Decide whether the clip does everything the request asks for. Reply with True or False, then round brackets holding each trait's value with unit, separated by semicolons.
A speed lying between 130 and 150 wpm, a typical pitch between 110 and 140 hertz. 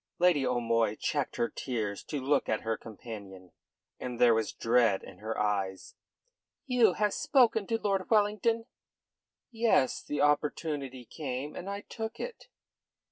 True (140 wpm; 135 Hz)